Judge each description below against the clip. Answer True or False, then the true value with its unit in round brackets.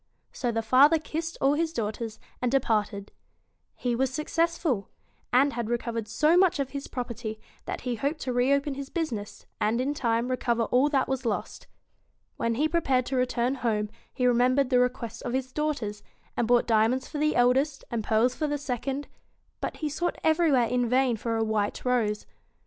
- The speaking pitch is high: True (250 Hz)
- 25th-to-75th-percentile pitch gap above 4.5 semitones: False (3.4 semitones)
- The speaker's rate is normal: True (190 wpm)